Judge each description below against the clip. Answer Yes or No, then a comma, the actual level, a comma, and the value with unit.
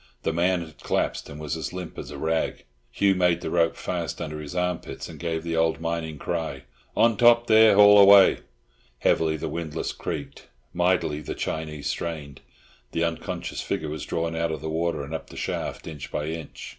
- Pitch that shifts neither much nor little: No, narrow, 2.3 semitones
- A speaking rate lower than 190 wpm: No, average, 195 wpm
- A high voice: No, very low, 80 Hz